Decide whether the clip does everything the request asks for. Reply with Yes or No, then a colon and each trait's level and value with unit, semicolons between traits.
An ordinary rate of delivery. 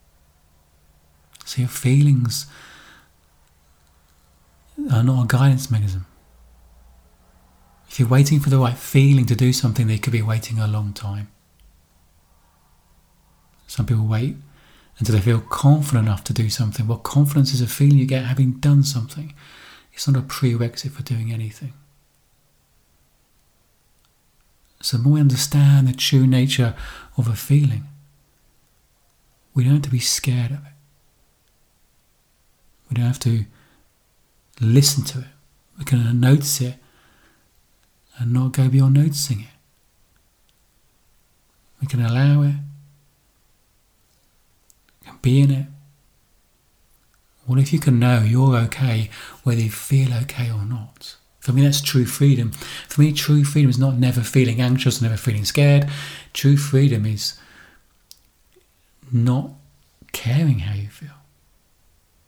No: slow, 130 wpm